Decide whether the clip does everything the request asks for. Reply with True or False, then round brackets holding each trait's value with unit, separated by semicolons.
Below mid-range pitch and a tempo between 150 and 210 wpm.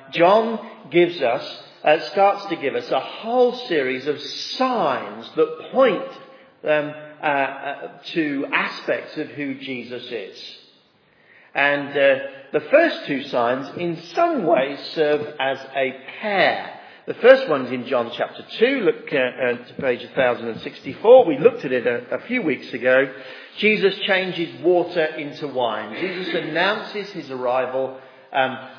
False (170 Hz; 155 wpm)